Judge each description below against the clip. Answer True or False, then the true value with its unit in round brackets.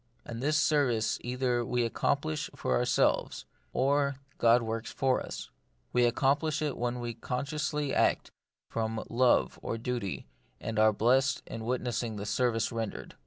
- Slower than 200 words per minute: True (150 wpm)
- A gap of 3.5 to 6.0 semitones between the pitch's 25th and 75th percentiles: False (2.9 semitones)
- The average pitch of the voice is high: False (120 Hz)